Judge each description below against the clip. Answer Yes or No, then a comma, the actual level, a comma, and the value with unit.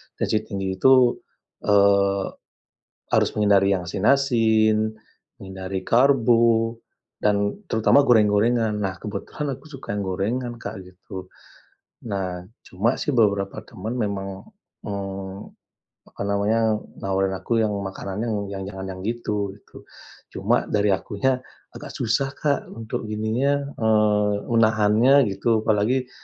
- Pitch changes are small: No, average, 3.0 semitones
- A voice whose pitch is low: Yes, low, 105 Hz